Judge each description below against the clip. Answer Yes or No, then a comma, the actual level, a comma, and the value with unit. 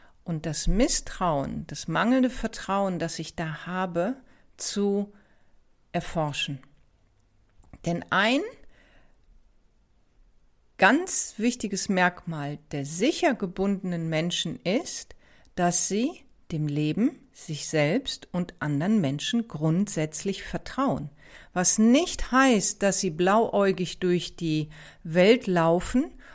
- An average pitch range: No, wide, 5.9 semitones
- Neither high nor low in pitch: Yes, medium, 180 Hz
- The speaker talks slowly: Yes, slow, 100 wpm